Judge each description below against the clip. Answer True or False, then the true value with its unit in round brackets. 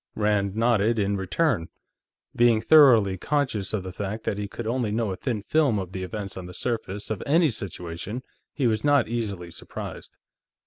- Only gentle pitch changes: False (3.6 semitones)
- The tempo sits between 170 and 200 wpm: True (180 wpm)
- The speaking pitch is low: True (110 Hz)